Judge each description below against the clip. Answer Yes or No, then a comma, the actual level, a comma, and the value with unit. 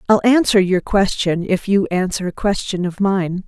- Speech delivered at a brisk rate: No, average, 190 wpm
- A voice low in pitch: No, high, 195 Hz